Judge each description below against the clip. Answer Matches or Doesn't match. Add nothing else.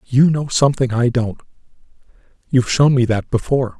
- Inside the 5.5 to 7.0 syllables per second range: Matches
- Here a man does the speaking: Matches